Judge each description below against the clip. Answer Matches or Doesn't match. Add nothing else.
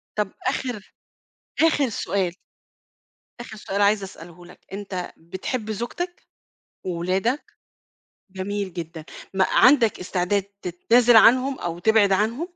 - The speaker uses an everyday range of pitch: Matches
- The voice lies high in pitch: Matches